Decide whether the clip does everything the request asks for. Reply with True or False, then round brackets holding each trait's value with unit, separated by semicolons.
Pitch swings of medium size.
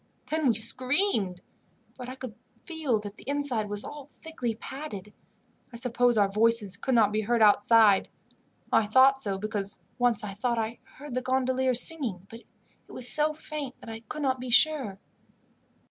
True (3.8 semitones)